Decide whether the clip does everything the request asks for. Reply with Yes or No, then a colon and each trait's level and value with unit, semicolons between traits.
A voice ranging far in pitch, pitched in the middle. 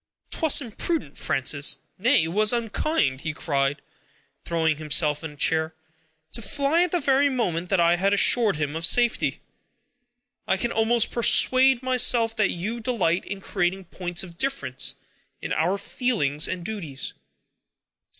No: wide, 7.0 semitones; high, 195 Hz